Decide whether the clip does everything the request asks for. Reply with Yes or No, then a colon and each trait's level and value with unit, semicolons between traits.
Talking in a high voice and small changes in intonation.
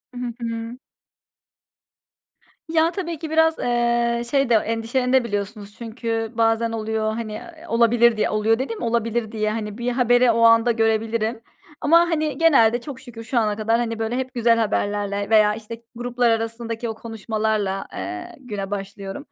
Yes: high, 230 Hz; narrow, 1.9 semitones